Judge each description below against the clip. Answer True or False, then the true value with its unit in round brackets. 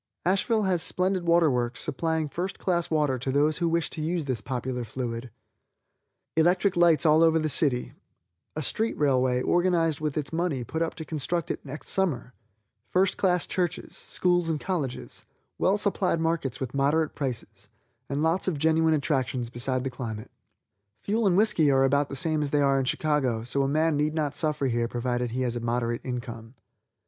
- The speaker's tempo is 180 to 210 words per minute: True (185 wpm)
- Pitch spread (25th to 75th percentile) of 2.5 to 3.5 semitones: False (4.6 semitones)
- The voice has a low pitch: False (150 Hz)